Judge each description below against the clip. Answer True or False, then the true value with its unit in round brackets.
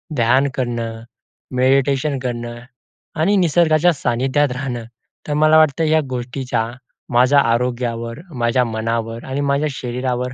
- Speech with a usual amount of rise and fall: True (3.2 semitones)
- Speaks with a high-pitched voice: False (125 Hz)